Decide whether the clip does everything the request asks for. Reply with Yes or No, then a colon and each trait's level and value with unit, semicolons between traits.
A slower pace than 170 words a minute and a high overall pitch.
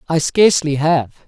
No: average, 140 wpm; medium, 165 Hz